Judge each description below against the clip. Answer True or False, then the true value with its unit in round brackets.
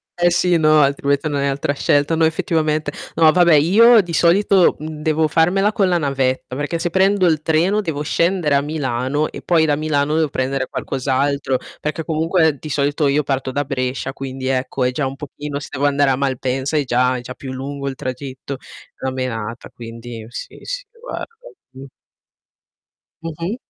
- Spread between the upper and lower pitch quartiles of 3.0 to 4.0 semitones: True (3.4 semitones)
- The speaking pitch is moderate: True (145 Hz)